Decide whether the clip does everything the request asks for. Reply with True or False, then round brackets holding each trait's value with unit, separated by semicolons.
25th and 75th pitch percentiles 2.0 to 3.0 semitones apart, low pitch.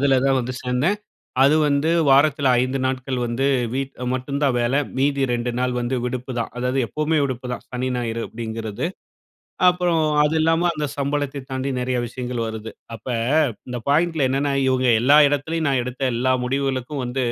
True (2.4 semitones; 130 Hz)